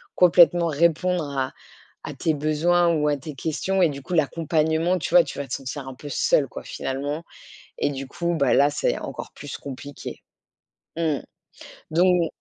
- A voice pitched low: No, medium, 155 Hz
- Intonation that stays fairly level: No, average, 3.2 semitones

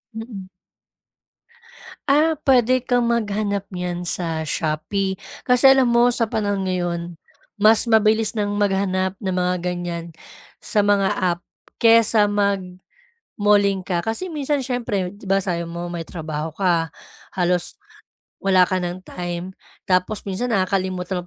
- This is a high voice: Yes, high, 195 Hz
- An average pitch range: Yes, average, 3.9 semitones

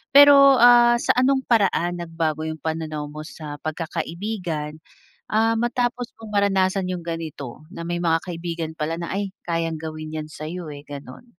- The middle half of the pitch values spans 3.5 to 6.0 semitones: Yes, average, 5.2 semitones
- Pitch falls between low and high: Yes, medium, 170 Hz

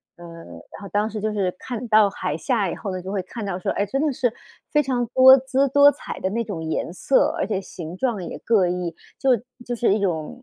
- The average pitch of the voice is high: Yes, high, 205 Hz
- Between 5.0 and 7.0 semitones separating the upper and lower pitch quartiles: Yes, average, 5.3 semitones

